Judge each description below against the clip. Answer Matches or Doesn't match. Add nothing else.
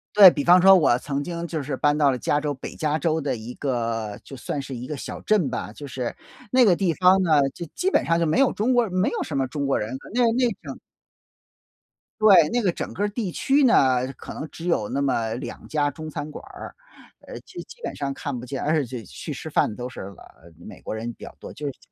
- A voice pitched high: Doesn't match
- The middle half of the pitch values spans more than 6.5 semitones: Doesn't match